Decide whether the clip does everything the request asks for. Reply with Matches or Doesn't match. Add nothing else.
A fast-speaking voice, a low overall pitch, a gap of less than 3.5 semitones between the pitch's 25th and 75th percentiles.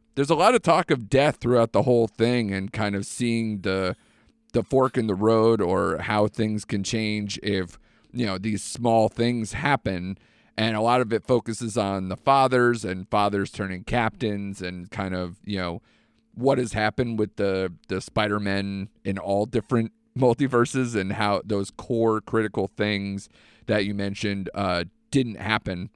Doesn't match